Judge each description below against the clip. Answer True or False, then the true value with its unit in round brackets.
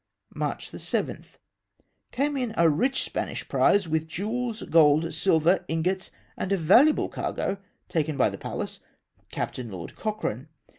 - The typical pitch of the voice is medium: True (170 Hz)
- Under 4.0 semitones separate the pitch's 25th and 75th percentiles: False (5.5 semitones)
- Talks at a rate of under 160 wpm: True (145 wpm)